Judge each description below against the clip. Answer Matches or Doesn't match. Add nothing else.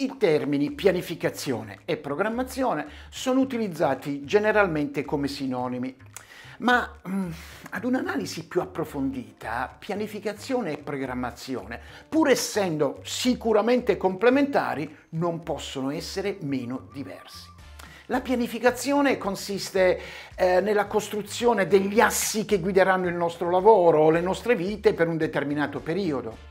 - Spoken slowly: Matches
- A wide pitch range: Matches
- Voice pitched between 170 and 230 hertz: Matches